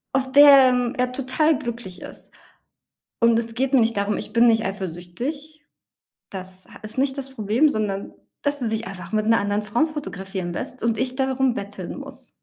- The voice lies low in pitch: No, high, 235 Hz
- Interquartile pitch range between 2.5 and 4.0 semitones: No, average, 4.6 semitones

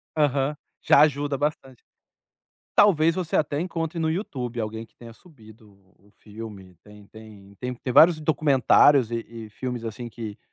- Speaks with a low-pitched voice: Yes, low, 125 Hz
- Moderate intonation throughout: No, wide, 5.7 semitones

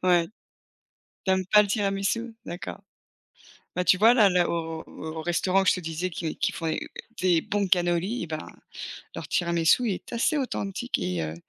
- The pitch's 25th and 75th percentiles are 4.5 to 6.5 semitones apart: No, average, 3.3 semitones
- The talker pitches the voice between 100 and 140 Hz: No, medium, 180 Hz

